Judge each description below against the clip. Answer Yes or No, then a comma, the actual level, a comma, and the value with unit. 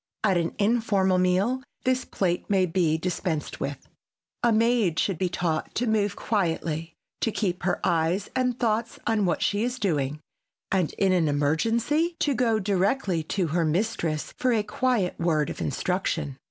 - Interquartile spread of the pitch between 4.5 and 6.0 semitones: Yes, average, 5.2 semitones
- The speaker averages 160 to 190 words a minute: Yes, average, 165 wpm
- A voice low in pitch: No, high, 190 Hz